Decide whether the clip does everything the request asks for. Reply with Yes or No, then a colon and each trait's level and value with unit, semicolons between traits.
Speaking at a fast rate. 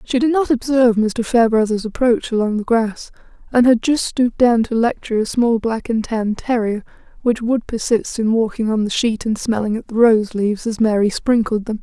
Yes: fast, 210 wpm